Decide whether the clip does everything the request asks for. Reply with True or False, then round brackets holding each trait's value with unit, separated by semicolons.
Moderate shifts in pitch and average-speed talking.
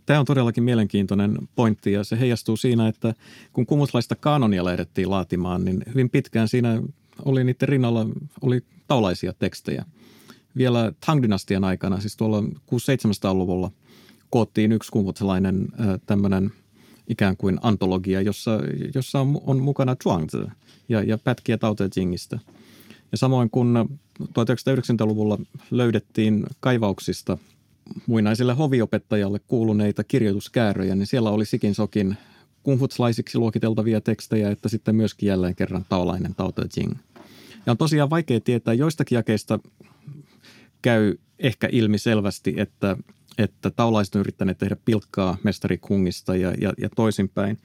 True (3.7 semitones; 130 wpm)